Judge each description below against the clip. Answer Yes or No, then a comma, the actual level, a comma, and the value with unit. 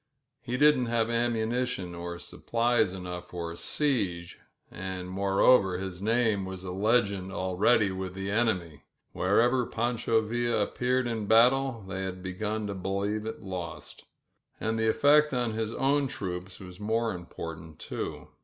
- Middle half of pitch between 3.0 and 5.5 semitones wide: Yes, average, 4.3 semitones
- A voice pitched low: Yes, low, 105 Hz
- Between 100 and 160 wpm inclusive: Yes, average, 150 wpm